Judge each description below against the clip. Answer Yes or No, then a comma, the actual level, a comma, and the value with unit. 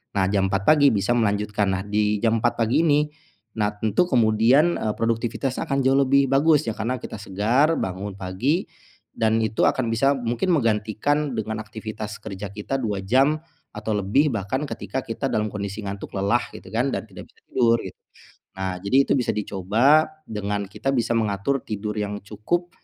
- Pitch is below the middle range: Yes, low, 110 Hz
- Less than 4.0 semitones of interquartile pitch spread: No, average, 4.5 semitones